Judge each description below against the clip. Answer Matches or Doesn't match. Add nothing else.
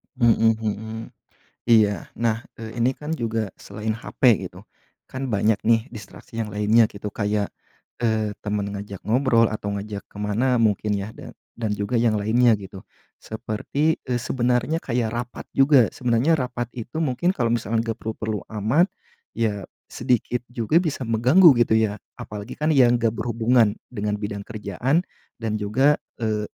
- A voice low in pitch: Matches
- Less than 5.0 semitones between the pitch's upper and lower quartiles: Matches